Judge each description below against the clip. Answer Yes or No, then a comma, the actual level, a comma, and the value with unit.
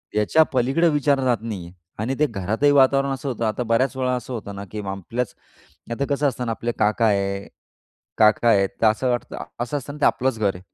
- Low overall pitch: Yes, low, 120 Hz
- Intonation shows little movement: No, average, 4.0 semitones